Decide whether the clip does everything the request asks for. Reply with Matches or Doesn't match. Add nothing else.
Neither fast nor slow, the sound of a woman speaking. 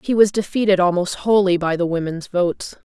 Matches